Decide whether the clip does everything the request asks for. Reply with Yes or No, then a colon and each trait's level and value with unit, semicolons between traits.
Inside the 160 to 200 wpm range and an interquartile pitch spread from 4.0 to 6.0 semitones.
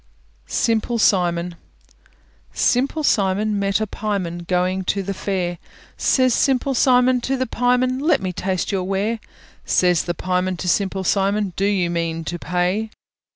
No: average, 150 wpm; average, 4.3 semitones